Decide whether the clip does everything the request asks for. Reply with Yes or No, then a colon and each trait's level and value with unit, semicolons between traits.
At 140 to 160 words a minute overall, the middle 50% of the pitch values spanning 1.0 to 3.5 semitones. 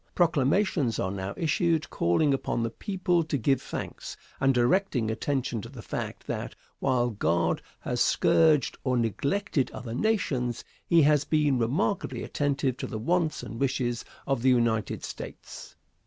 No: average, 150 wpm; average, 4.8 semitones